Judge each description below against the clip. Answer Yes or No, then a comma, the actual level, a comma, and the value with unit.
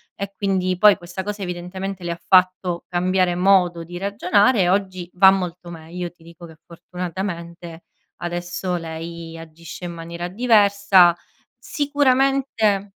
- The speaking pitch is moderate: Yes, medium, 180 Hz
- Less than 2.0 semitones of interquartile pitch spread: No, narrow, 2.4 semitones